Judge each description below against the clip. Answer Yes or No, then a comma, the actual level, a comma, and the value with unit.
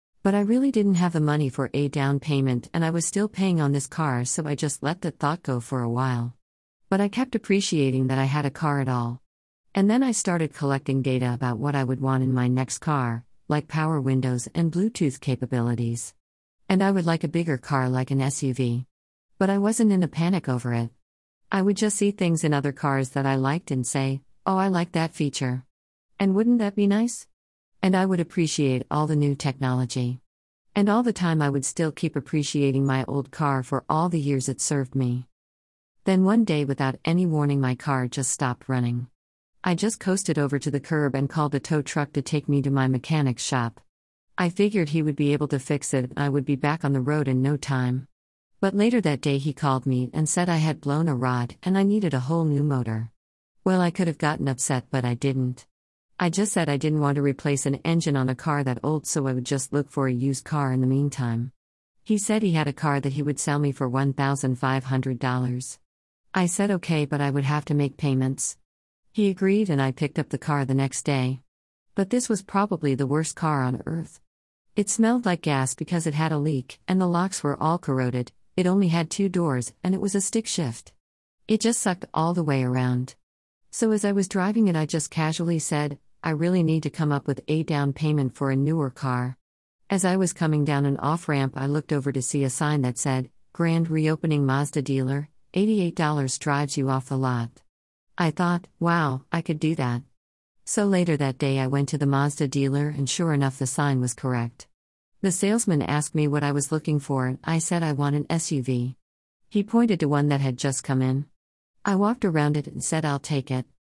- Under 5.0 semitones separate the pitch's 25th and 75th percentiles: Yes, average, 4.1 semitones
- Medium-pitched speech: Yes, medium, 145 Hz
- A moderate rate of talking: No, fast, 220 wpm